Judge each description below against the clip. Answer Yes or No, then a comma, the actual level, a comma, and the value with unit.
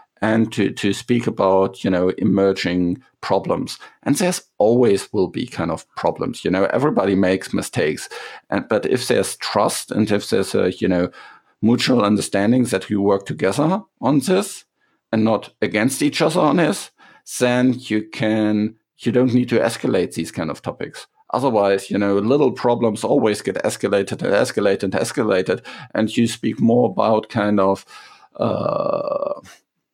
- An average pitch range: Yes, average, 3.9 semitones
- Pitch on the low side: Yes, low, 110 Hz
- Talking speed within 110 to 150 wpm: No, average, 160 wpm